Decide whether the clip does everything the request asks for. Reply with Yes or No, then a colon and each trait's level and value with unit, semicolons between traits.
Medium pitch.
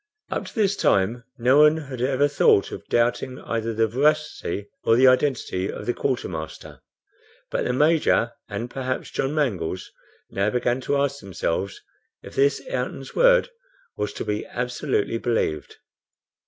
No: low, 125 Hz